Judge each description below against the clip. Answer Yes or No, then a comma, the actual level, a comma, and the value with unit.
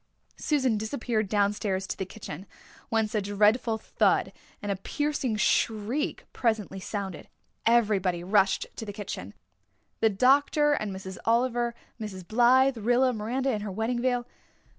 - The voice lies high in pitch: Yes, high, 220 Hz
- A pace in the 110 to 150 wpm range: Yes, average, 140 wpm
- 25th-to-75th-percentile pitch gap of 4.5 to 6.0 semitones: No, average, 3.4 semitones